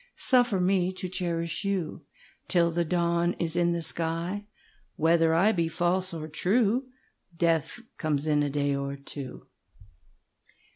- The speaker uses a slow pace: Yes, slow, 125 wpm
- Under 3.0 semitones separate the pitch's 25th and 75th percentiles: Yes, narrow, 2.5 semitones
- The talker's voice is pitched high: No, medium, 170 Hz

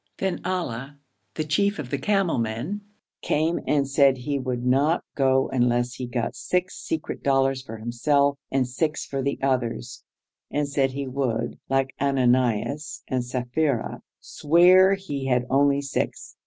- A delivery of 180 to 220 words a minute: No, average, 150 wpm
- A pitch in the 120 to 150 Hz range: Yes, low, 135 Hz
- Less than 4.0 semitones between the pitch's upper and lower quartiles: Yes, average, 3.1 semitones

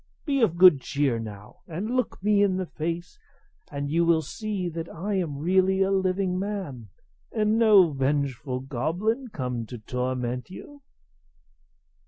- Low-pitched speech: No, medium, 170 Hz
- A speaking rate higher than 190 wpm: No, average, 150 wpm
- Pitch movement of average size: No, wide, 6.5 semitones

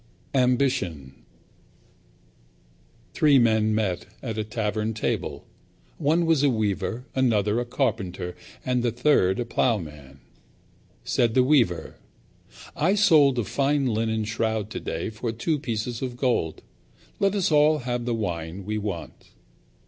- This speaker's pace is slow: Yes, slow, 130 wpm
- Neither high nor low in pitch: No, low, 115 Hz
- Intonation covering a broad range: No, average, 4.1 semitones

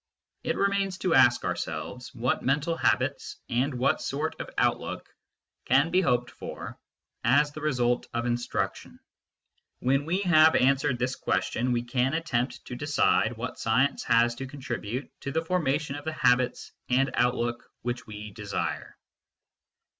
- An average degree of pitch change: Yes, average, 3.6 semitones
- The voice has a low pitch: Yes, low, 130 Hz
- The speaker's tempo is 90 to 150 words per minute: Yes, average, 145 wpm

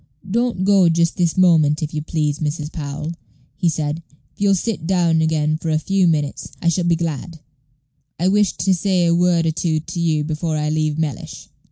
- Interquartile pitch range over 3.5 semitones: No, narrow, 2.6 semitones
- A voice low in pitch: No, medium, 165 Hz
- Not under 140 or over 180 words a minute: No, average, 200 wpm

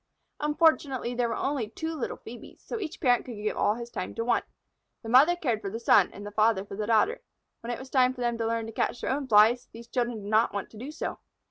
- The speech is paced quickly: Yes, fast, 260 wpm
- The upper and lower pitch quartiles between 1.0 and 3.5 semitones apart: Yes, average, 3.2 semitones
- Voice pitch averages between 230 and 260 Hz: Yes, high, 235 Hz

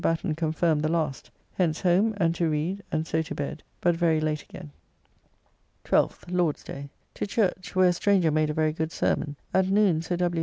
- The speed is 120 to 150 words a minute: No, average, 195 wpm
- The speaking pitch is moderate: Yes, medium, 165 Hz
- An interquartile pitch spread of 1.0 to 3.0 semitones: Yes, narrow, 2.5 semitones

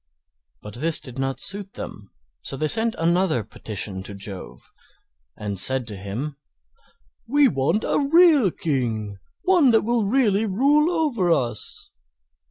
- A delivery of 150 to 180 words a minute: No, average, 140 wpm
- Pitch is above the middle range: No, medium, 165 Hz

